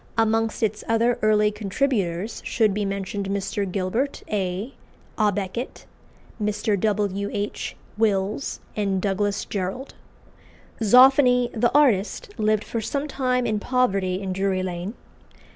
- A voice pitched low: No, high, 210 Hz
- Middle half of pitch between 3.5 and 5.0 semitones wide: No, average, 3.1 semitones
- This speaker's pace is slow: Yes, slow, 125 wpm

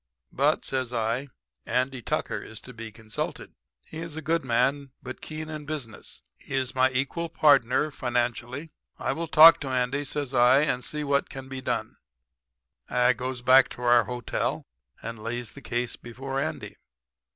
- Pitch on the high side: No, low, 130 Hz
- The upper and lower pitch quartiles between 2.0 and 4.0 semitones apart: Yes, average, 2.9 semitones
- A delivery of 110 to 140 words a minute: No, average, 170 wpm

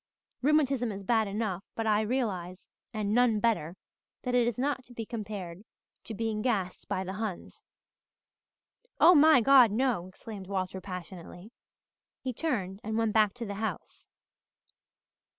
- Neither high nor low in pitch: No, high, 220 Hz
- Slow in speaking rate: No, average, 150 wpm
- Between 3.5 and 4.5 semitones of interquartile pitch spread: Yes, average, 4.0 semitones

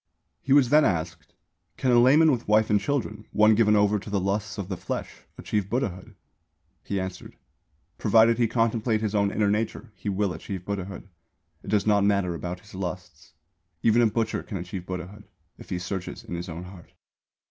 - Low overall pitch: Yes, low, 100 Hz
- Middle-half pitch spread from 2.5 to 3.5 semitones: Yes, average, 3.1 semitones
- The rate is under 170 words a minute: No, average, 185 wpm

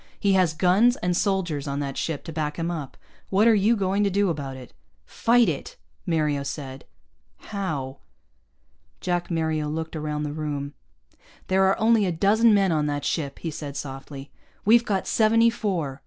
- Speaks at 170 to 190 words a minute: Yes, average, 175 wpm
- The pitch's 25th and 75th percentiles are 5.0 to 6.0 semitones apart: Yes, average, 5.3 semitones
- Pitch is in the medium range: Yes, medium, 165 Hz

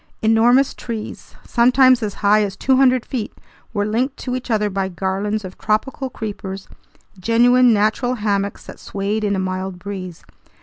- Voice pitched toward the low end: No, high, 215 Hz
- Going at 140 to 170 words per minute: Yes, average, 150 wpm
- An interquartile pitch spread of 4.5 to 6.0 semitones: No, average, 3.7 semitones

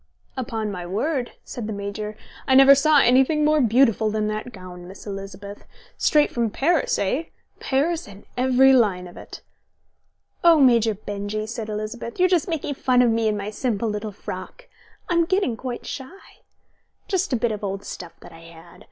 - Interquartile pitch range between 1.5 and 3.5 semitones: No, average, 4.7 semitones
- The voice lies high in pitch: Yes, high, 230 Hz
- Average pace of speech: Yes, average, 180 wpm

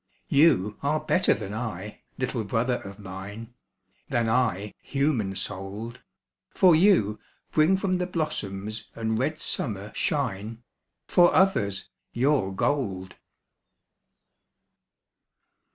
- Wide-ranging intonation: Yes, wide, 6.8 semitones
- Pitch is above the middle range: No, low, 115 Hz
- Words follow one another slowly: Yes, slow, 105 wpm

